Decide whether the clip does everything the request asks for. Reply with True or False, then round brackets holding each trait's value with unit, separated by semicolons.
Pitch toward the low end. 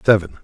True (100 Hz)